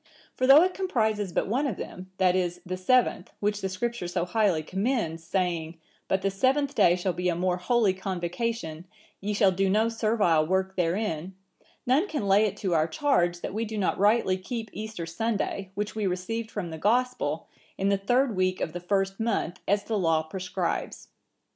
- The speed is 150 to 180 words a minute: No, average, 190 wpm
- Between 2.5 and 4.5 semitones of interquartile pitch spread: Yes, average, 3.9 semitones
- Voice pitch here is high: Yes, high, 195 Hz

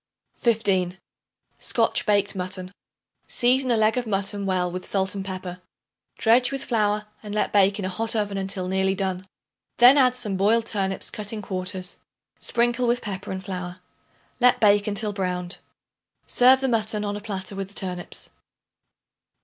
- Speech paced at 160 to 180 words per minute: Yes, average, 165 wpm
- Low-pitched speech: No, high, 200 Hz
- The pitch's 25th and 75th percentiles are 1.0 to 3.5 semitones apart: Yes, average, 3.0 semitones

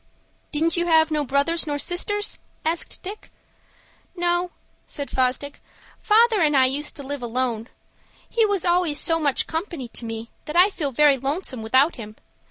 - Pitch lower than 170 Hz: No, very high, 300 Hz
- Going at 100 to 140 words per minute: No, average, 165 wpm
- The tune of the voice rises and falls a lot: No, average, 4.7 semitones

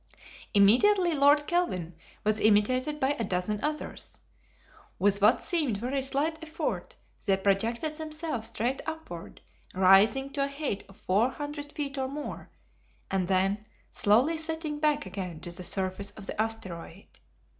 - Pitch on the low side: No, high, 240 Hz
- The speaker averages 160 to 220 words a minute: No, average, 145 wpm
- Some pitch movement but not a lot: No, wide, 7.0 semitones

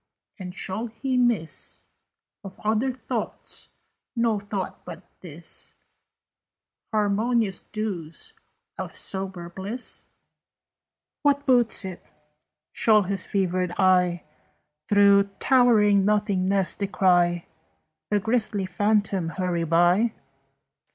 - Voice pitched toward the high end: Yes, high, 200 Hz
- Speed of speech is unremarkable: No, slow, 90 wpm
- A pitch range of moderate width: Yes, average, 3.1 semitones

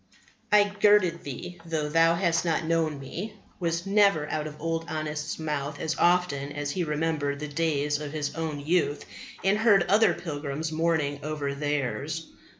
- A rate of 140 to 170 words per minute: Yes, average, 160 wpm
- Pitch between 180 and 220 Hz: No, medium, 160 Hz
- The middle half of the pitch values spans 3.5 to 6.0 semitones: No, narrow, 2.5 semitones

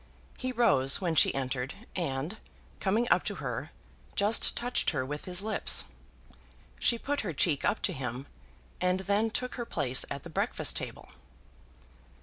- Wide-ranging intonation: Yes, wide, 8.2 semitones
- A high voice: No, medium, 180 Hz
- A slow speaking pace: No, average, 155 wpm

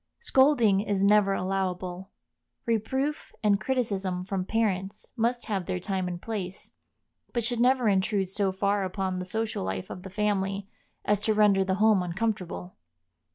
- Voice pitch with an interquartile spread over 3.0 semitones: No, average, 2.7 semitones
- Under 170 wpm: Yes, average, 155 wpm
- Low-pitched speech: No, high, 200 Hz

